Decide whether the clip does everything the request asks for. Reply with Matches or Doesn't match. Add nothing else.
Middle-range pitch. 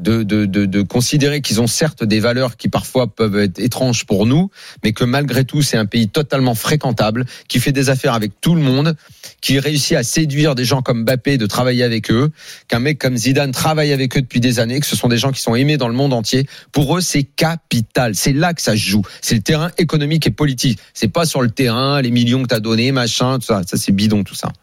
Doesn't match